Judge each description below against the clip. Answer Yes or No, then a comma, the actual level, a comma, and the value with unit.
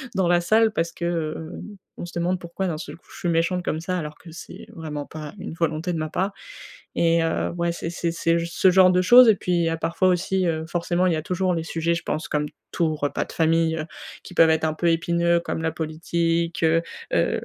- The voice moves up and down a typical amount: No, narrow, 1.7 semitones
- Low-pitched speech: No, medium, 170 Hz